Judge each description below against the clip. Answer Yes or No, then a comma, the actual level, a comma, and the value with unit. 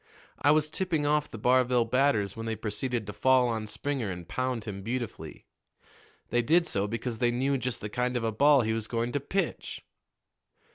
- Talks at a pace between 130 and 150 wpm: No, average, 195 wpm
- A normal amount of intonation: Yes, average, 3.6 semitones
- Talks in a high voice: No, low, 120 Hz